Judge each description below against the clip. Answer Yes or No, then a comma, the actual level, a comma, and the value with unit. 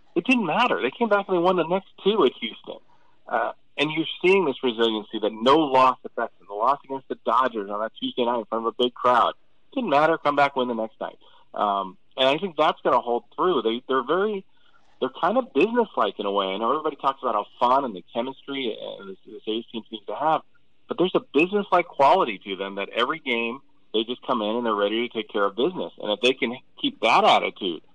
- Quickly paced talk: Yes, fast, 245 wpm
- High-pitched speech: No, low, 125 Hz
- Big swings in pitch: Yes, wide, 6.4 semitones